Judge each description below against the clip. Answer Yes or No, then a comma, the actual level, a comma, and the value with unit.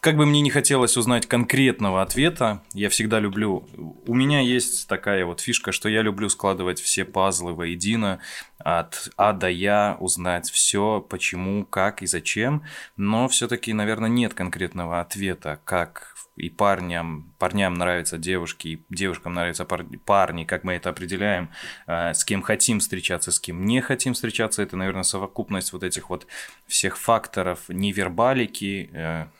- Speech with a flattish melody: No, average, 3.9 semitones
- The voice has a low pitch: Yes, very low, 95 Hz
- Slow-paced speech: No, average, 145 wpm